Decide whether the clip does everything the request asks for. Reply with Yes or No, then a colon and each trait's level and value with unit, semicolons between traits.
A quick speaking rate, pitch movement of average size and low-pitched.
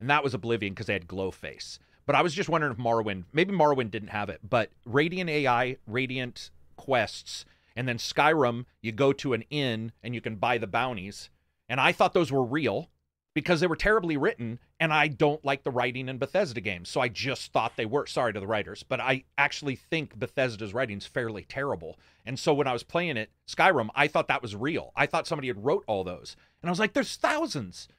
No: fast, 225 wpm; wide, 5.9 semitones; low, 125 Hz